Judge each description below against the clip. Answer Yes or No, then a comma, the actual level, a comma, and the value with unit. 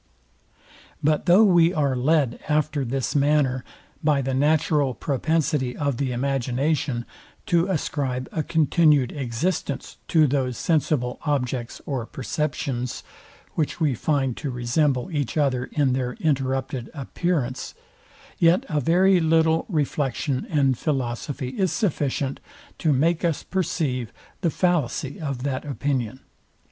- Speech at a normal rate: No, slow, 125 wpm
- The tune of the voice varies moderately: Yes, average, 3.5 semitones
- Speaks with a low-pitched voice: No, medium, 145 Hz